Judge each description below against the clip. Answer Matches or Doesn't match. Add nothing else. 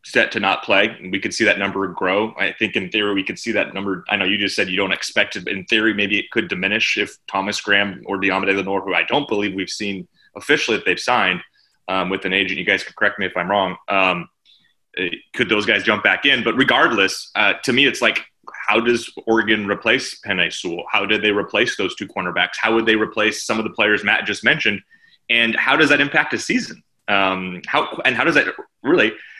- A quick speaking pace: Matches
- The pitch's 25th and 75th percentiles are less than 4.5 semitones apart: Matches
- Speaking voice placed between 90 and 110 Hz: Matches